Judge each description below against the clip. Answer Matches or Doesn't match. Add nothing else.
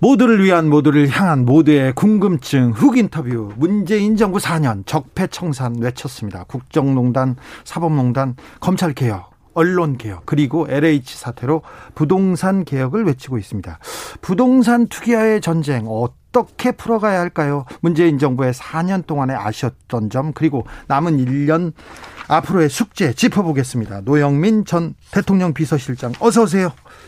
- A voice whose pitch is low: Doesn't match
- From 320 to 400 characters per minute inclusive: Doesn't match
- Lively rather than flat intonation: Matches